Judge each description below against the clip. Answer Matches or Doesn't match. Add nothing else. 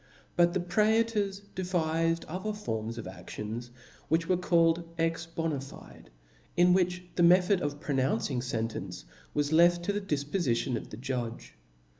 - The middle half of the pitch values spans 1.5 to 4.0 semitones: Doesn't match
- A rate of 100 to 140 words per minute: Matches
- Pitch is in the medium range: Matches